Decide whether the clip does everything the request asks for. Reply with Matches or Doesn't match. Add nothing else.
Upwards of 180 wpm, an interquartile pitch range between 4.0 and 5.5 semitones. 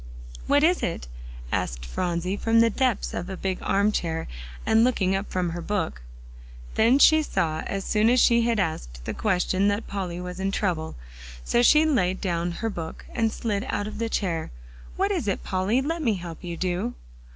Matches